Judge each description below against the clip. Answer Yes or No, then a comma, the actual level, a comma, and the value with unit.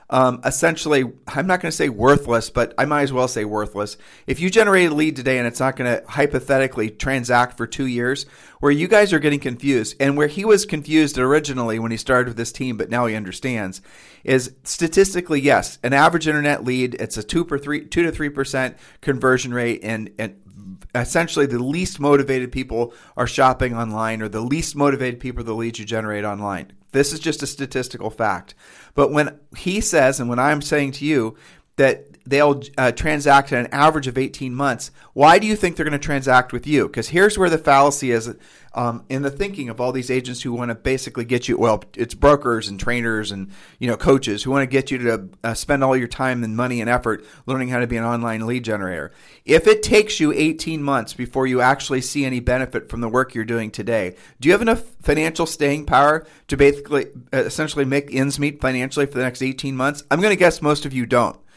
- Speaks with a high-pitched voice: No, low, 130 Hz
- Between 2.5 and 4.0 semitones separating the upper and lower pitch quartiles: Yes, average, 3.6 semitones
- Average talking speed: No, fast, 220 wpm